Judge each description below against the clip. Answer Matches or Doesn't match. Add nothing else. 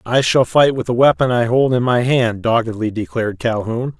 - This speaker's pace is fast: Matches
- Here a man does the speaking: Matches